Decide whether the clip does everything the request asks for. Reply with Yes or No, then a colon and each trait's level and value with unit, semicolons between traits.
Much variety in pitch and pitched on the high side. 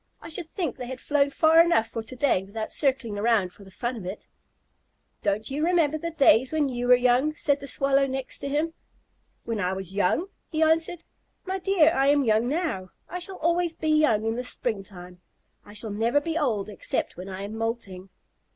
Yes: wide, 6.5 semitones; very high, 255 Hz